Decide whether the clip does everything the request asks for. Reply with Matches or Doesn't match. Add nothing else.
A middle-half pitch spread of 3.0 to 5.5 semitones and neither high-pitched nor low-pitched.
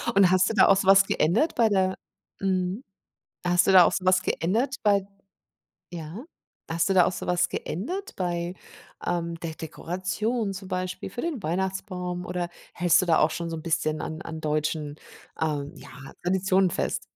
Doesn't match